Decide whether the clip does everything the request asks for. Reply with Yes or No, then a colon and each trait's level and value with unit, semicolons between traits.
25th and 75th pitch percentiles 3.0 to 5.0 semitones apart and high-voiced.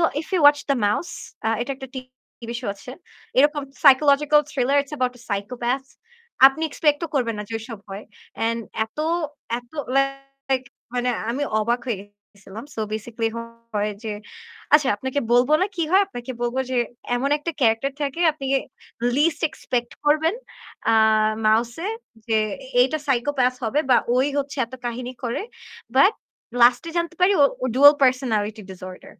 Yes: average, 3.7 semitones; very high, 255 Hz